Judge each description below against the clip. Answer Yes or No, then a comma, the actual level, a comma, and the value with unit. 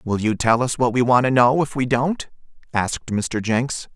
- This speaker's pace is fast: Yes, fast, 230 wpm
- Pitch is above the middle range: No, low, 125 Hz